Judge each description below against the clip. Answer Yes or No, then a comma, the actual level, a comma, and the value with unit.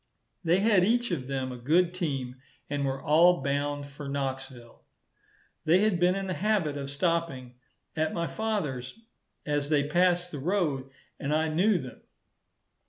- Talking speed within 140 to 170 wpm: Yes, average, 160 wpm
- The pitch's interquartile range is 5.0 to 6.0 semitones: No, average, 4.6 semitones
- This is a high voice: No, medium, 155 Hz